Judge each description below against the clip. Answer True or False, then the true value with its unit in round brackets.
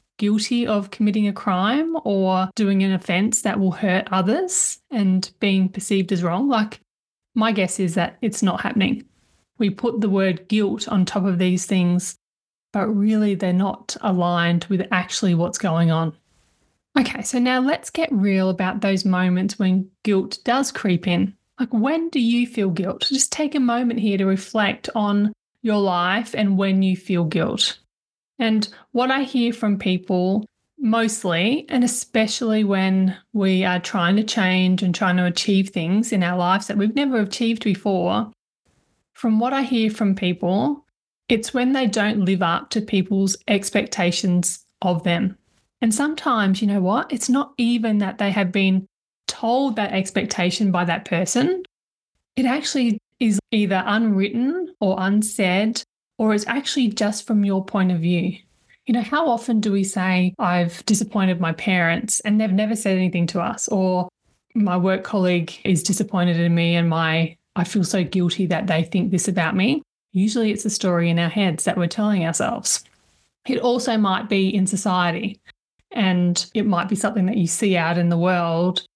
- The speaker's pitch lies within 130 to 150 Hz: False (200 Hz)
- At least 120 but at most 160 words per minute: False (170 wpm)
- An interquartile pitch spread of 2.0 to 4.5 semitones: True (3.4 semitones)